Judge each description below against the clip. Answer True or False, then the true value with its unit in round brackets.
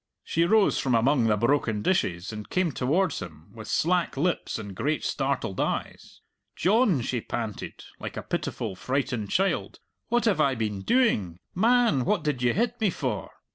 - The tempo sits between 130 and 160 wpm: False (170 wpm)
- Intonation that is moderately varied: False (9.0 semitones)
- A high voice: False (135 Hz)